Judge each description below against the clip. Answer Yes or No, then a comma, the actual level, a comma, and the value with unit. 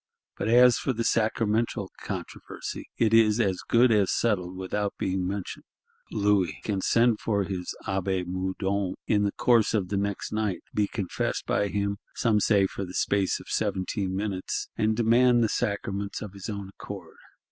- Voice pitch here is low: Yes, low, 100 Hz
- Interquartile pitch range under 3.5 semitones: Yes, narrow, 2.5 semitones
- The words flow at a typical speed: Yes, average, 165 wpm